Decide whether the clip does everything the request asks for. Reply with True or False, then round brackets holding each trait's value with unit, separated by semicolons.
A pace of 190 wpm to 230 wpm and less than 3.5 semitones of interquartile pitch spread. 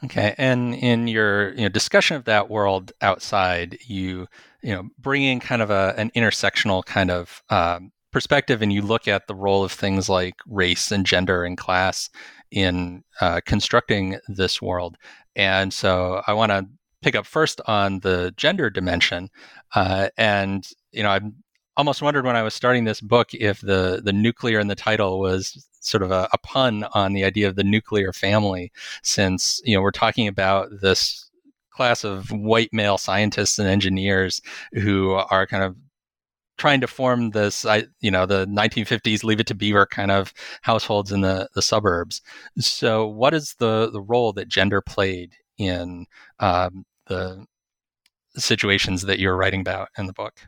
False (175 wpm; 3.0 semitones)